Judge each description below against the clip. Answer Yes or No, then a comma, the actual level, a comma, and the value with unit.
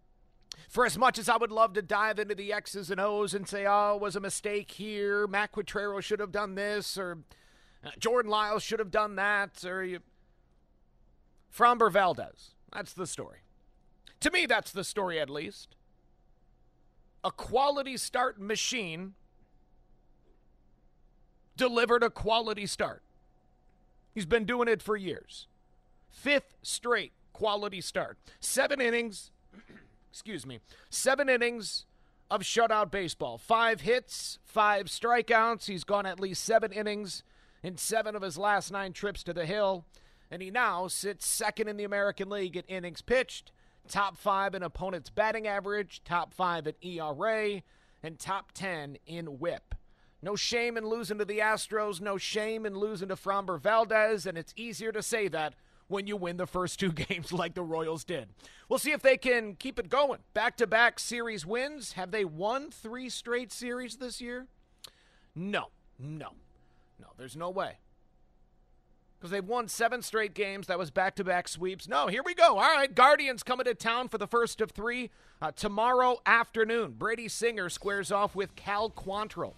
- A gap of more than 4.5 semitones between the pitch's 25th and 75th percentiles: No, average, 3.6 semitones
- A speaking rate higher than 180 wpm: No, average, 165 wpm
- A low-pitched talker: No, high, 205 Hz